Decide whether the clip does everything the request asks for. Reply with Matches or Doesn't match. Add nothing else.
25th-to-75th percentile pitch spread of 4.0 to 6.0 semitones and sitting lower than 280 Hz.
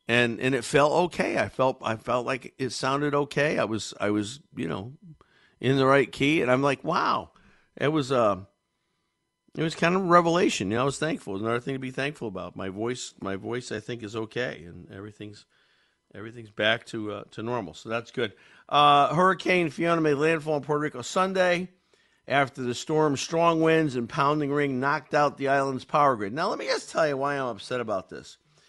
Matches